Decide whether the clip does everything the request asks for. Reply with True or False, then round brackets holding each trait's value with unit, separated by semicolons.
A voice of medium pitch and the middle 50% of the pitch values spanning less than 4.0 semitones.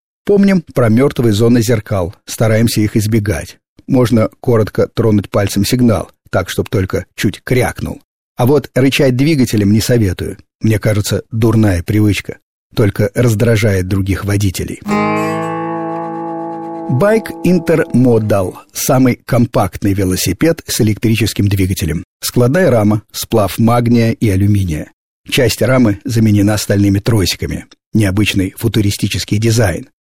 False (110 Hz; 3.6 semitones)